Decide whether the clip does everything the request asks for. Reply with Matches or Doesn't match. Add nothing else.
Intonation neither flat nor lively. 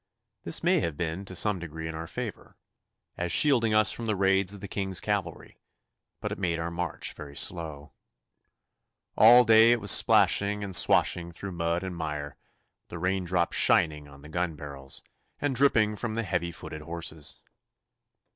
Matches